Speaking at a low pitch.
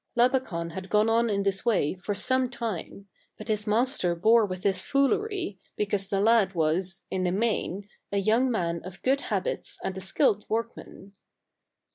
No: high, 205 Hz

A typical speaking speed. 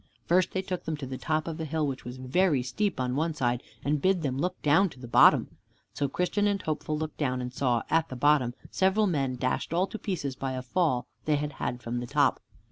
No: fast, 245 wpm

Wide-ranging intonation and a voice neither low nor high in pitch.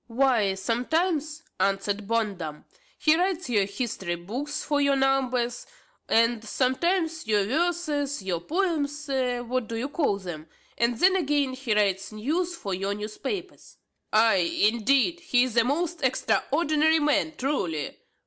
No: wide, 6.2 semitones; very high, 255 Hz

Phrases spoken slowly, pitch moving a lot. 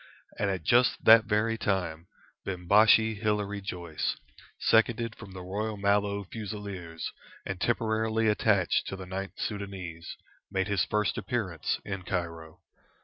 No: slow, 130 wpm; average, 2.9 semitones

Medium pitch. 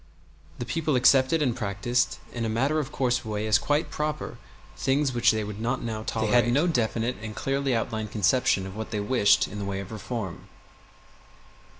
No: low, 120 Hz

